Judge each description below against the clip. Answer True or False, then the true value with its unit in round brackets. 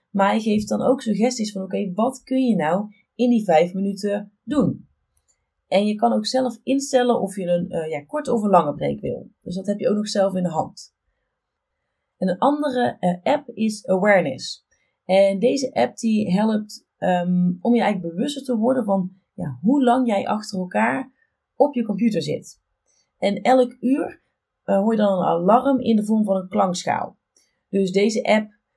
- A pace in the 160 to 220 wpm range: True (195 wpm)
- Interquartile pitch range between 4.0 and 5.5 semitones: True (4.4 semitones)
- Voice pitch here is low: False (210 Hz)